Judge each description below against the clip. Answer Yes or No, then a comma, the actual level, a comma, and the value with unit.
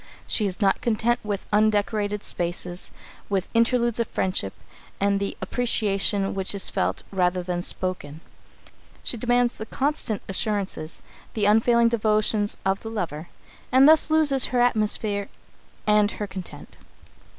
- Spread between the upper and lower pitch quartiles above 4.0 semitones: No, average, 3.3 semitones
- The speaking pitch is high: Yes, high, 210 Hz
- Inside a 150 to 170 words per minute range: No, slow, 135 wpm